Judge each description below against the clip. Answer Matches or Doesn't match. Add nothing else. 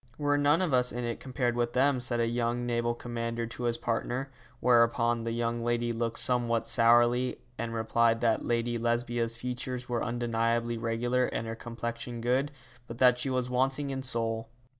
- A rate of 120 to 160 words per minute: Doesn't match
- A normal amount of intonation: Doesn't match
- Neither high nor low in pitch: Doesn't match